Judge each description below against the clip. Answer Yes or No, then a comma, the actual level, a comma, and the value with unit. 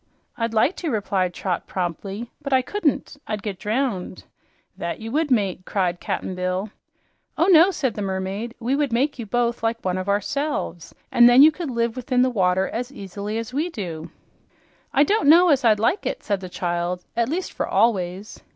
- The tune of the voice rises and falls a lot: Yes, wide, 6.0 semitones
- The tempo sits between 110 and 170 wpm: No, average, 195 wpm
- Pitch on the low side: No, high, 225 Hz